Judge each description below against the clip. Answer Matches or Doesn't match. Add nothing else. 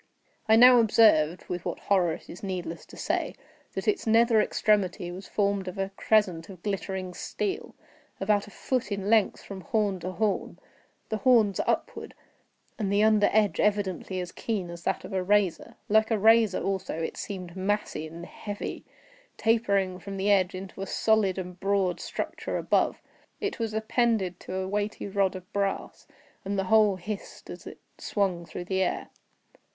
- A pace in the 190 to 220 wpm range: Doesn't match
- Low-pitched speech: Doesn't match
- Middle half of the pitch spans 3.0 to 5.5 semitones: Doesn't match